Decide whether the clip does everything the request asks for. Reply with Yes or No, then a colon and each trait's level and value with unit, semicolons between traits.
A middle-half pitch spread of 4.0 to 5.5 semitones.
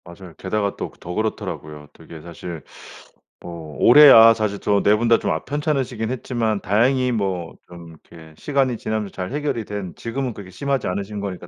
Yes: average, 5.2 semitones